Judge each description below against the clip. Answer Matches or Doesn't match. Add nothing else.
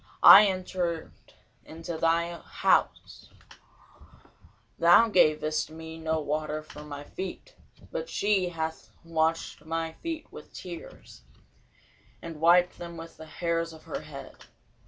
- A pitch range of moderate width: Doesn't match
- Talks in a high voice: Doesn't match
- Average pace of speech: Doesn't match